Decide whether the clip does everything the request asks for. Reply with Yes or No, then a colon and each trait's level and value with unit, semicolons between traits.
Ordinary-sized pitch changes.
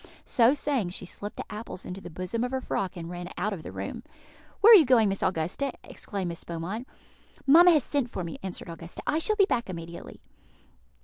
No: wide, 7.0 semitones